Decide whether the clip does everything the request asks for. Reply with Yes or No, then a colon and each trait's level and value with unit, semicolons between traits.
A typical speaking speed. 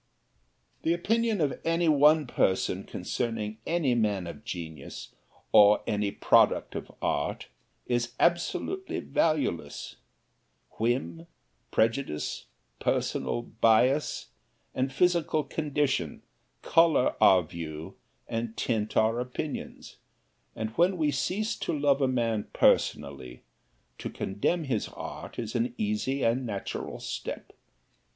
No: slow, 110 wpm